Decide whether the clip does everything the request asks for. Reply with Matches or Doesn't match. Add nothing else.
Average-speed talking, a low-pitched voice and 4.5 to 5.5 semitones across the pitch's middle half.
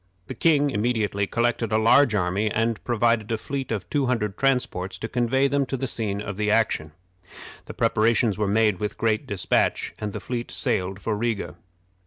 Doesn't match